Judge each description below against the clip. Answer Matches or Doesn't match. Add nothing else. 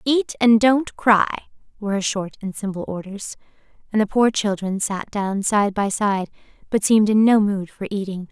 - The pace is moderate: Matches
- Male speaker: Doesn't match